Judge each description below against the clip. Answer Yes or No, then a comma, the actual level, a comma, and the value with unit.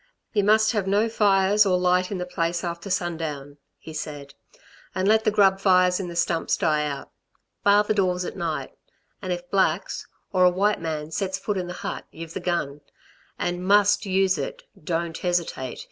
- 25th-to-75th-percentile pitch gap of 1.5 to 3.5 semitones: Yes, average, 2.9 semitones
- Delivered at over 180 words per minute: Yes, average, 190 wpm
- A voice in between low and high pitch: Yes, medium, 180 Hz